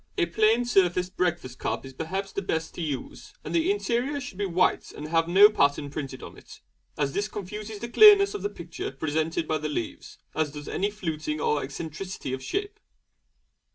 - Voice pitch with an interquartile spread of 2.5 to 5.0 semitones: No, wide, 5.6 semitones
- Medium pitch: Yes, medium, 175 Hz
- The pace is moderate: Yes, average, 190 wpm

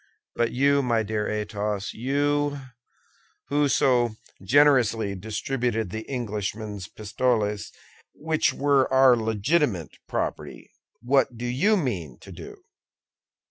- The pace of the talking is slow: Yes, slow, 100 wpm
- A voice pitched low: Yes, low, 120 Hz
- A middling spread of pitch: Yes, average, 4.7 semitones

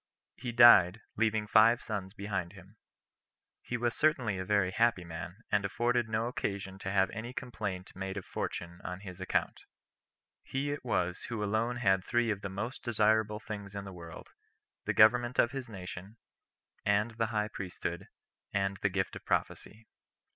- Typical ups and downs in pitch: Yes, average, 3.4 semitones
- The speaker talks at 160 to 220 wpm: Yes, average, 170 wpm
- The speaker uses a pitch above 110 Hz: No, low, 105 Hz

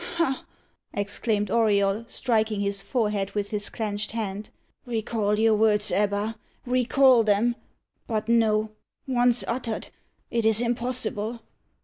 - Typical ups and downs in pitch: No, narrow, 2.2 semitones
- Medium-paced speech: No, slow, 115 wpm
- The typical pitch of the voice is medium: No, high, 220 Hz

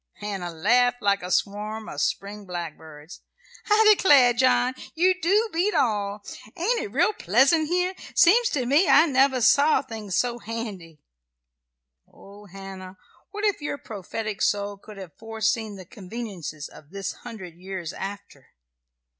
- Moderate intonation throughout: No, wide, 6.1 semitones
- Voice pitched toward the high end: Yes, high, 220 Hz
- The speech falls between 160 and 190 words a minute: No, average, 145 wpm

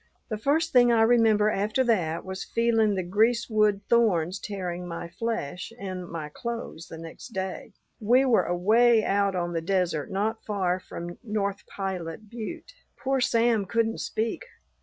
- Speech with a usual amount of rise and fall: Yes, average, 4.3 semitones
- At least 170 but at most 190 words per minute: No, average, 150 wpm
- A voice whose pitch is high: Yes, high, 210 Hz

